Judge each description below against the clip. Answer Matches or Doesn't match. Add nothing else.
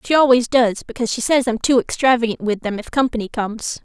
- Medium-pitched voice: Doesn't match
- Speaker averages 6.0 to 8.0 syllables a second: Matches